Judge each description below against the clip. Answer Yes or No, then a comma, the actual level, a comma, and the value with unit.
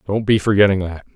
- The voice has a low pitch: Yes, low, 100 Hz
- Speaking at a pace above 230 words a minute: No, fast, 205 wpm